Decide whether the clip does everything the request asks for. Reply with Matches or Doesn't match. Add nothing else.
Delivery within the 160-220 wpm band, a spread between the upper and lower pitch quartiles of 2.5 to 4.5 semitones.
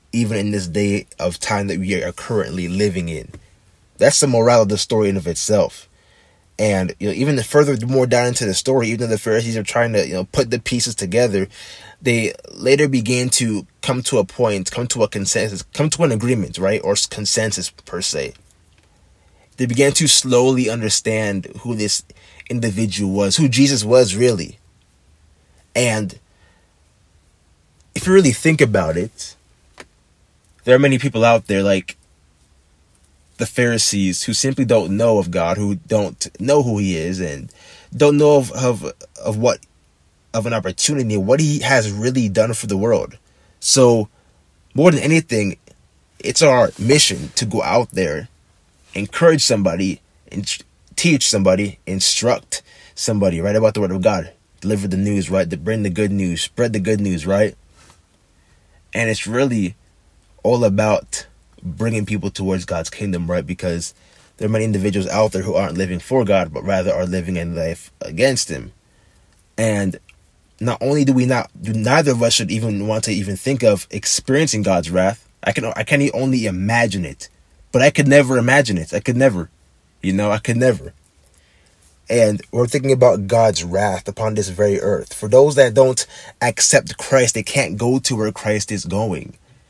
Doesn't match